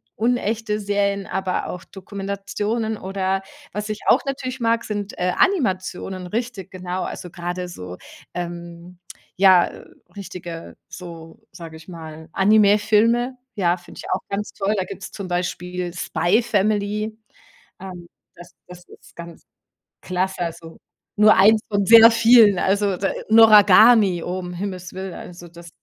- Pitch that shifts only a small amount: No, average, 3.0 semitones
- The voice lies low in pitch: No, high, 190 Hz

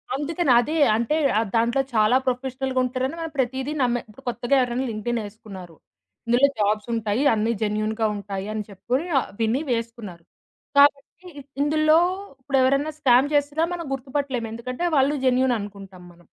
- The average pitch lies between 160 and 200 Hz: No, high, 245 Hz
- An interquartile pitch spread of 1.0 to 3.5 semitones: No, average, 4.1 semitones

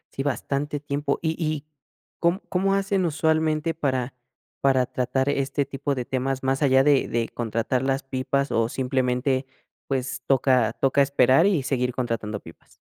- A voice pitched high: No, low, 135 Hz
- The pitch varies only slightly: Yes, narrow, 2.3 semitones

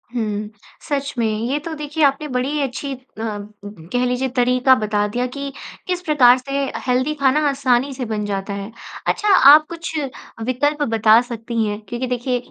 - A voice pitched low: No, very high, 250 Hz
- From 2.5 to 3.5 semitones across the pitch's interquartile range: No, average, 4.1 semitones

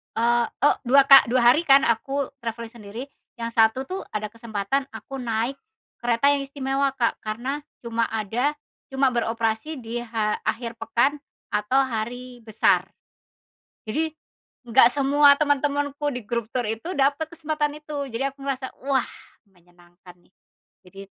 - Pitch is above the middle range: Yes, very high, 250 Hz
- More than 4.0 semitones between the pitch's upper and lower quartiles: No, average, 3.6 semitones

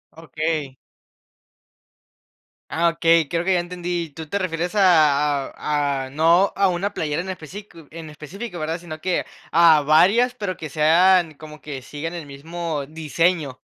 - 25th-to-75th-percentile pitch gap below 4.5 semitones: Yes, average, 2.7 semitones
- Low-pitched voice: No, medium, 165 Hz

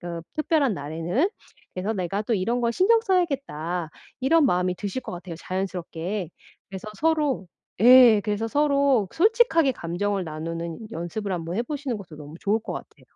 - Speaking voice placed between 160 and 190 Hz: No, high, 205 Hz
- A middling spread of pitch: No, wide, 7.8 semitones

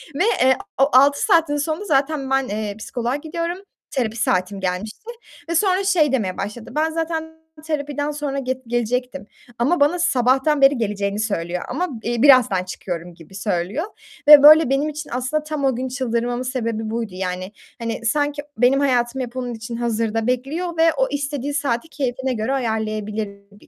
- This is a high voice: Yes, very high, 255 Hz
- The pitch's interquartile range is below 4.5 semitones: No, average, 4.9 semitones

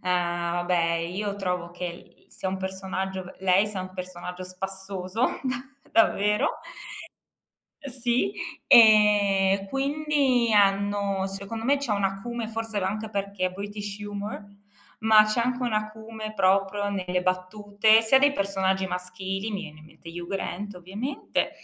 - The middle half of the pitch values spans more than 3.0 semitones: No, narrow, 2.5 semitones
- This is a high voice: Yes, high, 200 Hz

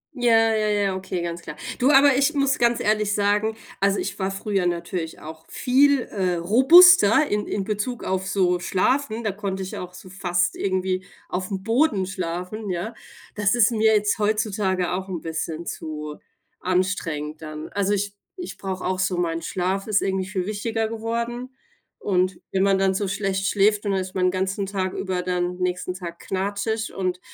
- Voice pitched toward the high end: Yes, high, 195 Hz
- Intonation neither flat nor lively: Yes, average, 3.0 semitones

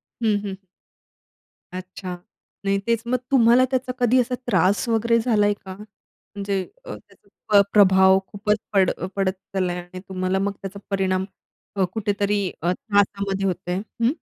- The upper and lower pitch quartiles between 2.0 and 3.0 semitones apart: Yes, narrow, 2.6 semitones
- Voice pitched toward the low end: No, high, 200 Hz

